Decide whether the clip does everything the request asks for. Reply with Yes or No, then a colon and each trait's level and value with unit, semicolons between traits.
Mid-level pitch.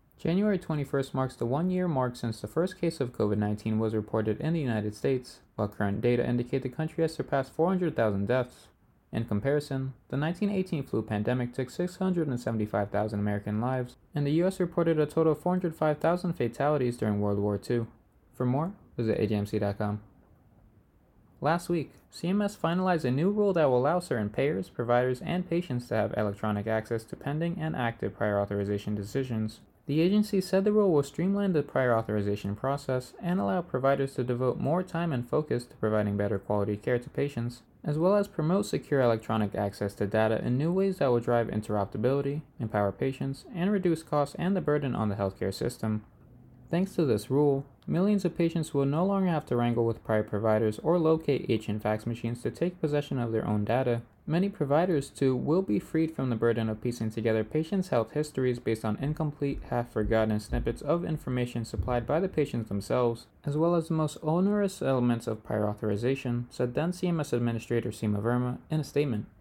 No: low, 125 Hz